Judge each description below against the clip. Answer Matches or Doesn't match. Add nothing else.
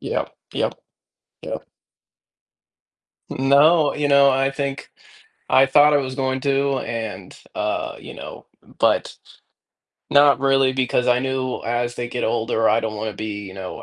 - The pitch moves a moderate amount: Matches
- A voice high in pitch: Doesn't match